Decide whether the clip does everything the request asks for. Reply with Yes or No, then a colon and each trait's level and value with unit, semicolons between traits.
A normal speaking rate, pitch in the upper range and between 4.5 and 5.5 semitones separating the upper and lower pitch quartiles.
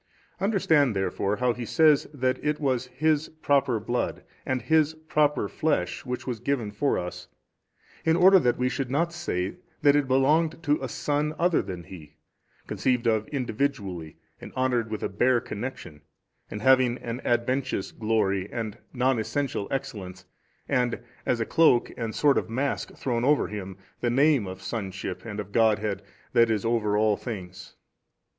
No: average, 165 wpm; low, 125 Hz; average, 5.2 semitones